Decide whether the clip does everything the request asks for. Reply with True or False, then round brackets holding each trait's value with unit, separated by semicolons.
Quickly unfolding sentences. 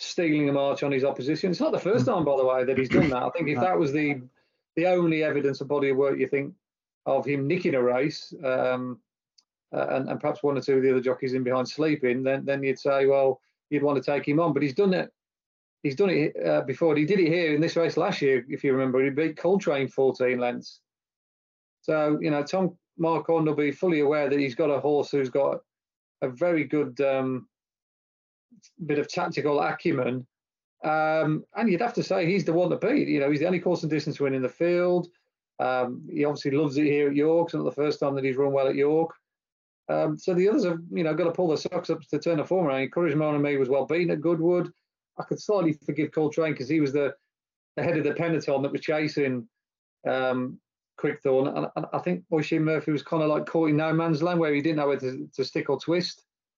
True (240 wpm)